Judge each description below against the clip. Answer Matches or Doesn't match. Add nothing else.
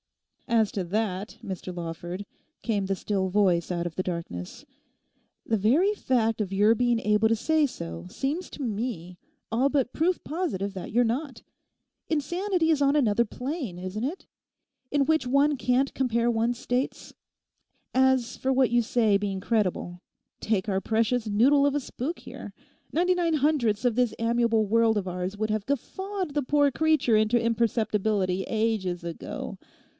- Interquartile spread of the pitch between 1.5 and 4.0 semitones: Doesn't match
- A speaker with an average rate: Matches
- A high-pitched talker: Matches